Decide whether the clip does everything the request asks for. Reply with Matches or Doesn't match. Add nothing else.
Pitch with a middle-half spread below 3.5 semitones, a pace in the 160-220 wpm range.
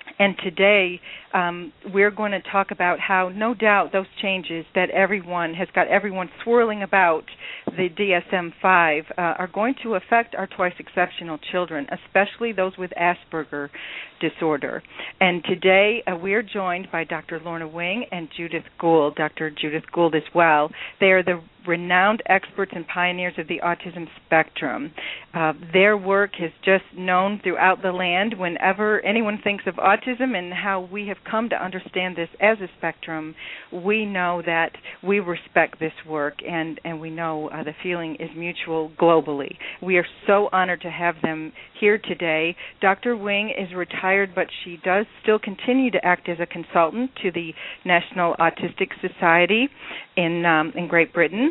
Matches